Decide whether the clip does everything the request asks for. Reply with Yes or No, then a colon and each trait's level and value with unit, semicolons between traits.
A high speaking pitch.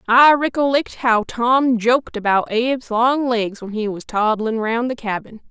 Yes: high, 235 Hz